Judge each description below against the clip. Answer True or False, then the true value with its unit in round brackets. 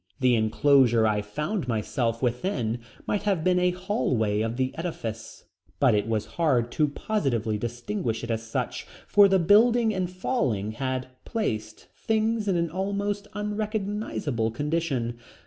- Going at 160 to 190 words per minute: False (145 wpm)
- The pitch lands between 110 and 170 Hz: True (140 Hz)